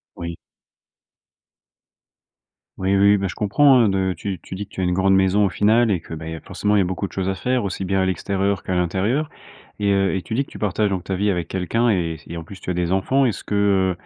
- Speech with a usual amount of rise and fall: No, narrow, 2.1 semitones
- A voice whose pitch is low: Yes, very low, 95 Hz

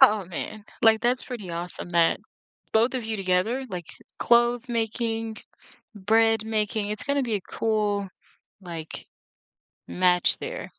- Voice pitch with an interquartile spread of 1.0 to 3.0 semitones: No, average, 3.7 semitones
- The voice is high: Yes, high, 220 Hz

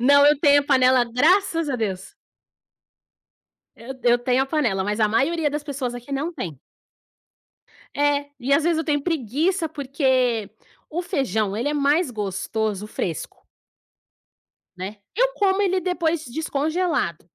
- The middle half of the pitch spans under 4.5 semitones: No, wide, 5.4 semitones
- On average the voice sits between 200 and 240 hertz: No, very high, 280 Hz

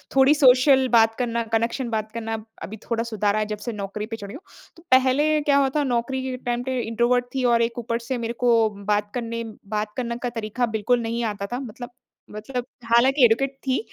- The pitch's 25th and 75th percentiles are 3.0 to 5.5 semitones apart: No, narrow, 2.6 semitones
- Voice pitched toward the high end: Yes, high, 235 Hz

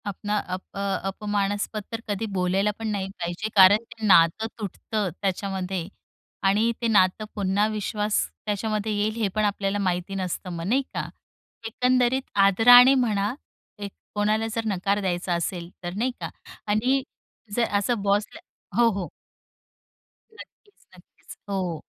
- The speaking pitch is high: Yes, high, 205 Hz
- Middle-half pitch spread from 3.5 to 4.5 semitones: No, narrow, 2.4 semitones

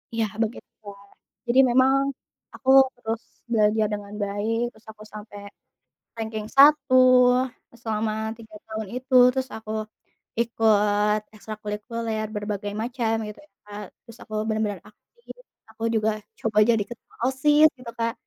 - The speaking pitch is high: Yes, high, 220 Hz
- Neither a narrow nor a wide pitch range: No, narrow, 2.2 semitones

